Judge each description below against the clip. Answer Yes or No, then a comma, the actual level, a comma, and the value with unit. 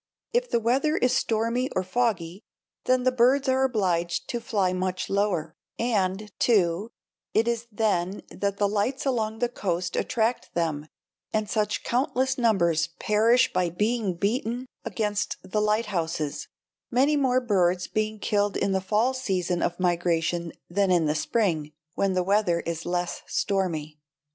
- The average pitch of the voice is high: Yes, high, 205 Hz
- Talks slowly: No, average, 150 wpm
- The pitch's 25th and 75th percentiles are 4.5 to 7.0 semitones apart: Yes, average, 5.0 semitones